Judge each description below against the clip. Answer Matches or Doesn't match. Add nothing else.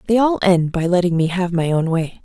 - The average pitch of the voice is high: Doesn't match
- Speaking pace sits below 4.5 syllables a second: Doesn't match